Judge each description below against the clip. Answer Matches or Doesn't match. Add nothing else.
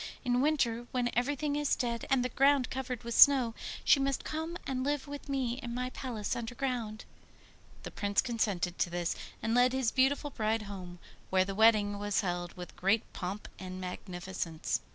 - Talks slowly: Doesn't match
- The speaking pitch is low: Doesn't match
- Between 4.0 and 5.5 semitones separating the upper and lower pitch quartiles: Matches